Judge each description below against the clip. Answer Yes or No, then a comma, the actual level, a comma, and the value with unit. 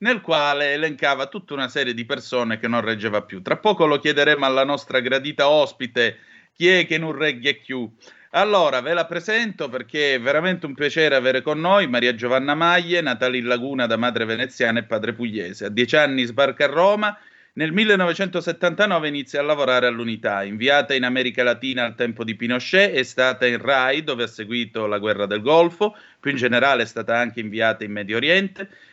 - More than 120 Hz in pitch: Yes, low, 135 Hz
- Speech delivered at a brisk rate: Yes, fast, 190 wpm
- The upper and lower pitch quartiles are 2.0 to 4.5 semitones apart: No, average, 5.1 semitones